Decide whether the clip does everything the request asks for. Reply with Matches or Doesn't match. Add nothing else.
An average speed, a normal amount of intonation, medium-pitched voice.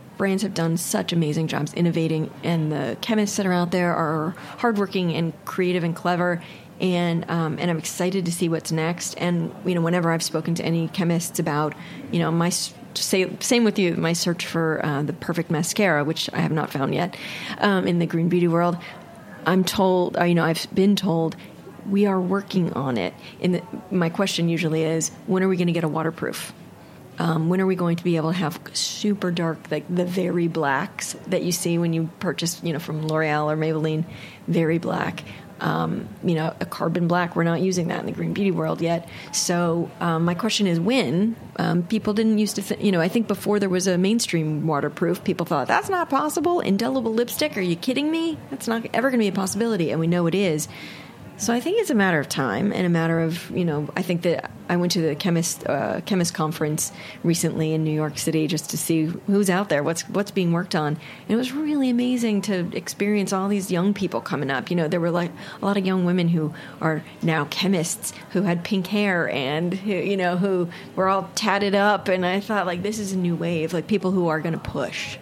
Doesn't match